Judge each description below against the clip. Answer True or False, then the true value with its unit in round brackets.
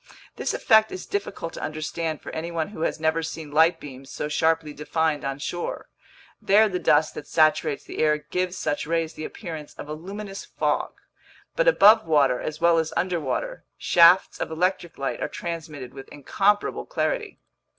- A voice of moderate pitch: True (160 Hz)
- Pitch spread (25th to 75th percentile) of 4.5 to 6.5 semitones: False (3.3 semitones)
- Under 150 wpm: False (170 wpm)